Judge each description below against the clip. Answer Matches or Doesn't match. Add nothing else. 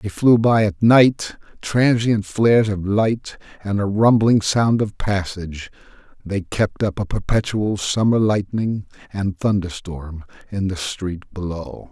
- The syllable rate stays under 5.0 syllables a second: Matches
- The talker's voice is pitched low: Matches